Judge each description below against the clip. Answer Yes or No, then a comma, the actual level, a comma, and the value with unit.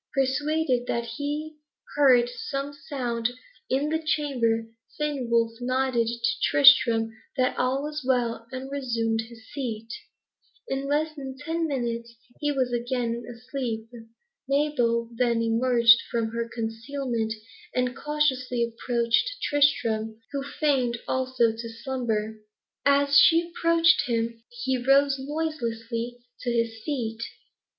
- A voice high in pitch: Yes, very high, 250 Hz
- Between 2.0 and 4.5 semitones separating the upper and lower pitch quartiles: Yes, average, 3.4 semitones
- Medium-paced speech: No, slow, 120 wpm